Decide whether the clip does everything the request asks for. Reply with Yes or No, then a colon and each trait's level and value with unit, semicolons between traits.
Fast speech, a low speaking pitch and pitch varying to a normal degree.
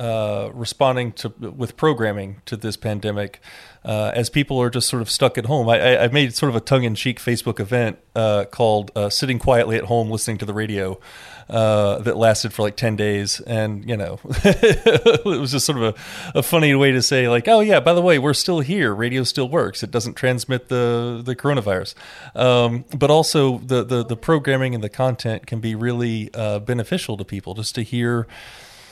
Yes: fast, 210 wpm; low, 120 Hz; average, 3.1 semitones